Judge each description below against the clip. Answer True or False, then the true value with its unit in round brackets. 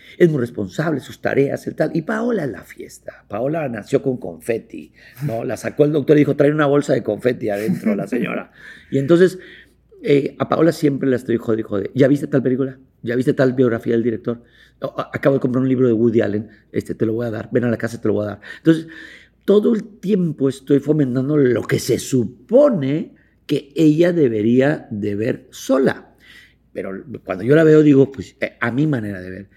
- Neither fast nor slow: False (205 wpm)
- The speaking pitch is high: False (135 Hz)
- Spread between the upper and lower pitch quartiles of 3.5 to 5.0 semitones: True (4.7 semitones)